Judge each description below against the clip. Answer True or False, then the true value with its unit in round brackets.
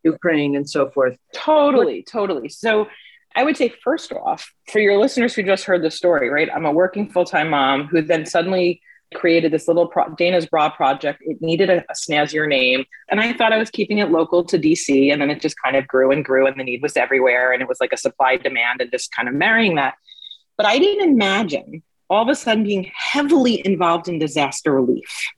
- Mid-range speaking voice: True (175 Hz)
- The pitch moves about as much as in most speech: False (6.4 semitones)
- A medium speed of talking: False (220 wpm)